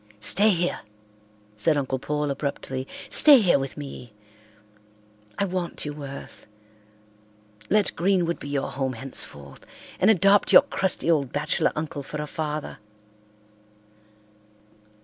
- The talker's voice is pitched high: No, medium, 150 Hz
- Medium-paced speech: No, slow, 120 wpm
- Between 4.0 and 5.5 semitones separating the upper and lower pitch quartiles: Yes, average, 4.5 semitones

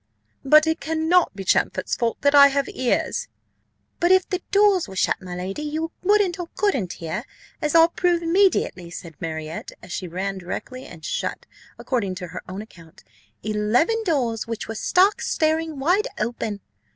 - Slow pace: No, average, 170 wpm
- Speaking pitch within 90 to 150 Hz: No, very high, 270 Hz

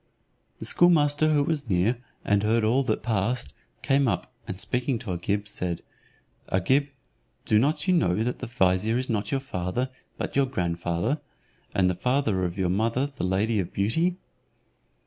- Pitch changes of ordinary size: No, wide, 6.3 semitones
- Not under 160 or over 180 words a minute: Yes, average, 165 wpm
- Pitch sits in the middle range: No, low, 110 Hz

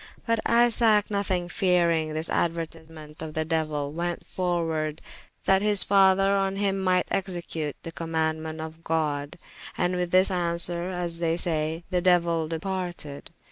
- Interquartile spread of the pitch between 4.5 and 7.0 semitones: No, average, 2.7 semitones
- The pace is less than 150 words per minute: Yes, average, 140 wpm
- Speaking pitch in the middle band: Yes, medium, 170 Hz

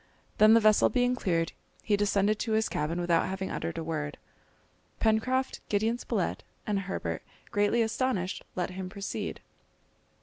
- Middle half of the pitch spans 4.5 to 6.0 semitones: No, average, 3.7 semitones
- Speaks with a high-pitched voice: Yes, high, 205 Hz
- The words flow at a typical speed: Yes, average, 145 wpm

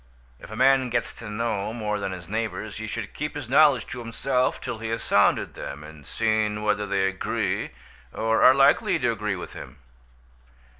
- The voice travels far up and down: No, average, 2.7 semitones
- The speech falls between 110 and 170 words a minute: No, average, 190 wpm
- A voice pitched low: Yes, low, 110 Hz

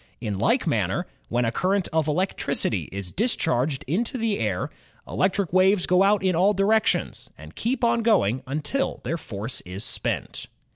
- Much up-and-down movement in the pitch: Yes, wide, 8.6 semitones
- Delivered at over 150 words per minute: Yes, average, 160 wpm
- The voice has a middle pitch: Yes, medium, 180 Hz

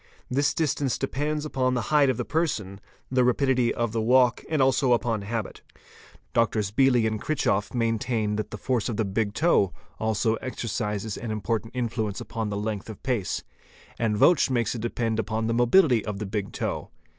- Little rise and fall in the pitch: No, average, 3.1 semitones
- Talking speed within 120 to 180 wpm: No, average, 190 wpm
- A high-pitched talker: No, low, 115 Hz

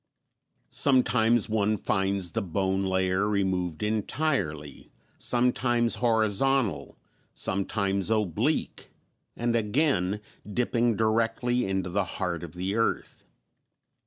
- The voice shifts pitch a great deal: No, average, 3.8 semitones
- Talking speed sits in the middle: No, slow, 95 wpm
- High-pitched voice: No, low, 105 Hz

